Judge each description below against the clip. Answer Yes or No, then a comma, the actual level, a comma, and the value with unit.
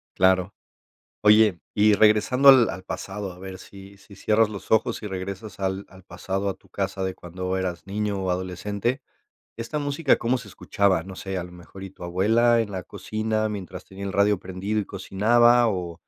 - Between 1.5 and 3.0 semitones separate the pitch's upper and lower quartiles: Yes, narrow, 2.5 semitones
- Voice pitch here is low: Yes, low, 100 Hz